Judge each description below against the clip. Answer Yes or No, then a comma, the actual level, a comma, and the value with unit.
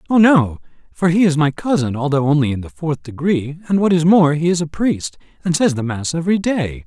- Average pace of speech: No, fast, 235 wpm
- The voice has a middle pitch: Yes, medium, 155 Hz